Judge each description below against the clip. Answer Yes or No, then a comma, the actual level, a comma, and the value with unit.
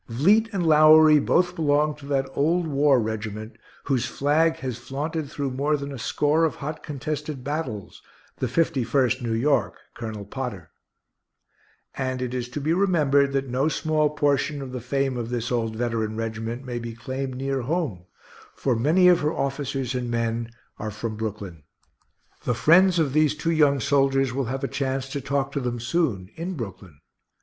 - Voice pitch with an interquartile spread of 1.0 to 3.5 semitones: No, average, 4.2 semitones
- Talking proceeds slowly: No, average, 175 wpm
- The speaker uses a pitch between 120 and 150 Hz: Yes, low, 135 Hz